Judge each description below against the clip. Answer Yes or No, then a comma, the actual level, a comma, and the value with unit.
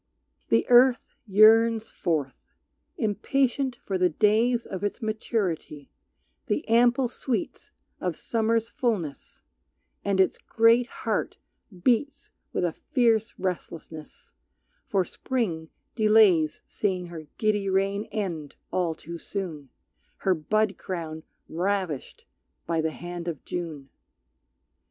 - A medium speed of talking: No, slow, 110 wpm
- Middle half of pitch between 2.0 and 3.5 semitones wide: No, average, 5.2 semitones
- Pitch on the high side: Yes, high, 200 Hz